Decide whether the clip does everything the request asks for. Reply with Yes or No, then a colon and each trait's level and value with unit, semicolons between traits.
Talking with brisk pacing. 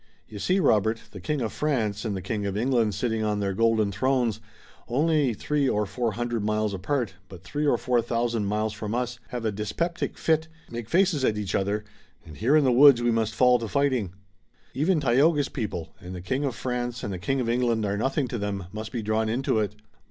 Yes: fast, 220 wpm